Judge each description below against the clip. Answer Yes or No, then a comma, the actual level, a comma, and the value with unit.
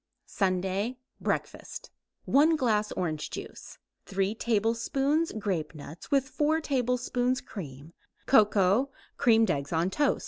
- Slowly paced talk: Yes, slow, 105 wpm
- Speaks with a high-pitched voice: Yes, high, 220 Hz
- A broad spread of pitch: Yes, wide, 5.9 semitones